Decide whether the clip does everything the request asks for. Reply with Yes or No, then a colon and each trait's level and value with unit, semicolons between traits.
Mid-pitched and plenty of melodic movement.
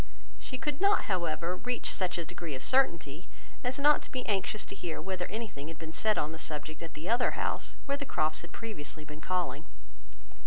Yes: medium, 180 Hz; wide, 7.0 semitones